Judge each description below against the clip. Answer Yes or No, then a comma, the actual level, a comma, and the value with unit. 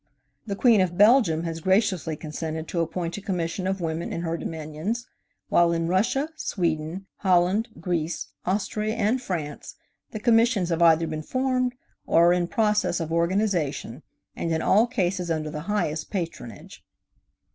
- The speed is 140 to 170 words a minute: Yes, average, 155 wpm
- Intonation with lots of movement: No, average, 4.2 semitones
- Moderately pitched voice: Yes, medium, 175 Hz